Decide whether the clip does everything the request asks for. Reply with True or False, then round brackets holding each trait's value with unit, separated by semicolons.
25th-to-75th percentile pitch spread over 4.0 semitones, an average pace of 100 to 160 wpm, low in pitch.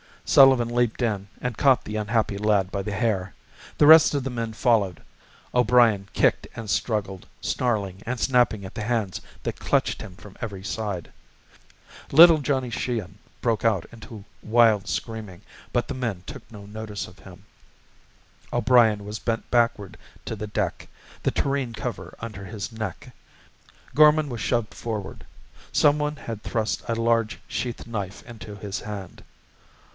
False (3.0 semitones; 155 wpm; 110 Hz)